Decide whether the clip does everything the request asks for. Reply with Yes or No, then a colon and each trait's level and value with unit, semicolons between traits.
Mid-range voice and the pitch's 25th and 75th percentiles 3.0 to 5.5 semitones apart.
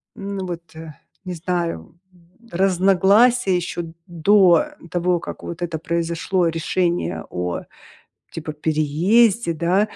No: medium, 175 Hz; narrow, 2.5 semitones